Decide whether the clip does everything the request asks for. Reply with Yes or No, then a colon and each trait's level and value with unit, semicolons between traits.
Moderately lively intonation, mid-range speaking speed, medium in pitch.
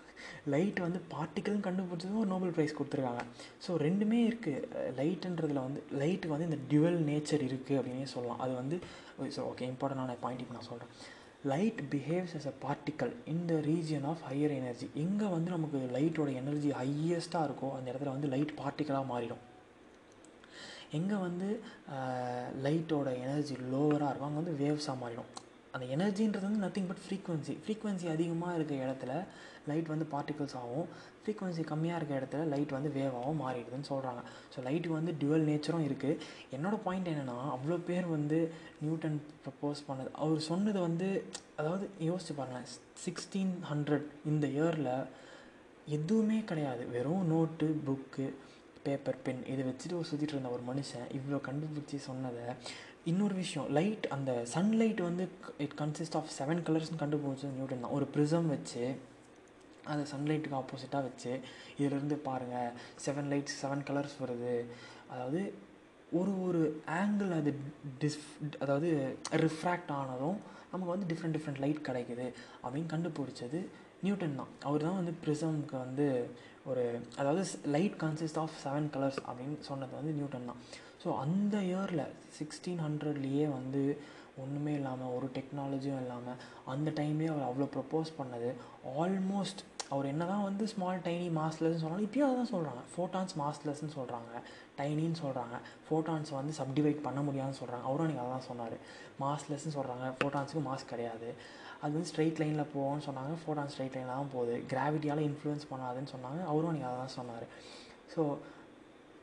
No: average, 3.5 semitones; fast, 145 wpm; medium, 150 Hz